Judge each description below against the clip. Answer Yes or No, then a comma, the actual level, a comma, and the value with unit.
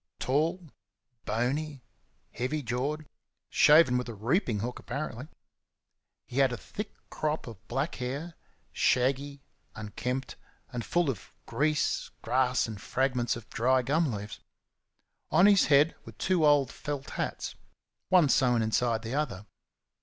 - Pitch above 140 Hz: No, low, 130 Hz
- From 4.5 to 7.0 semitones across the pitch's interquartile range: No, average, 4.0 semitones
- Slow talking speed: Yes, slow, 130 wpm